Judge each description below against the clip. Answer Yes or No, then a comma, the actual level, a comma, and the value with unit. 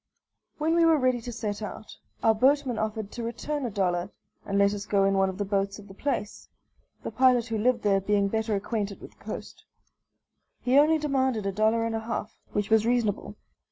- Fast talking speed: Yes, fast, 210 wpm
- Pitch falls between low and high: No, high, 220 Hz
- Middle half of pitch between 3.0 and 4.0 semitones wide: Yes, average, 3.7 semitones